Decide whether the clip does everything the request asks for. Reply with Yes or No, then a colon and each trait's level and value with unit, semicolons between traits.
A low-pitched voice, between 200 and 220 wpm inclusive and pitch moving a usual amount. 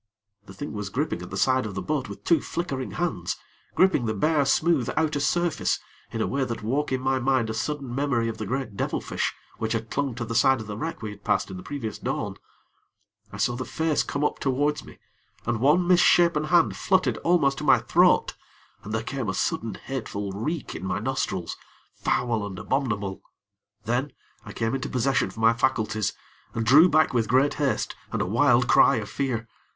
Yes: low, 130 Hz; fast, 205 wpm; average, 4.7 semitones